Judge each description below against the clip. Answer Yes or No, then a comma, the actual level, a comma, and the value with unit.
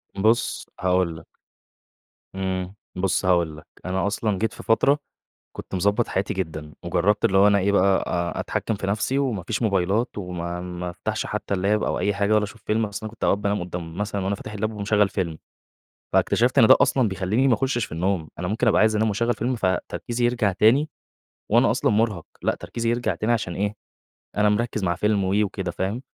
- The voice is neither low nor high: No, low, 100 Hz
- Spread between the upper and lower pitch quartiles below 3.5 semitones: Yes, average, 2.9 semitones